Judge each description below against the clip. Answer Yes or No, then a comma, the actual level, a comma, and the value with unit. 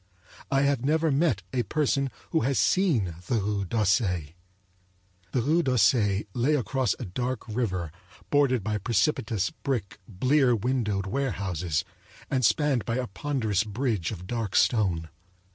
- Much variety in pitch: Yes, wide, 5.7 semitones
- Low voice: Yes, low, 115 Hz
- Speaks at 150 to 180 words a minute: No, slow, 135 wpm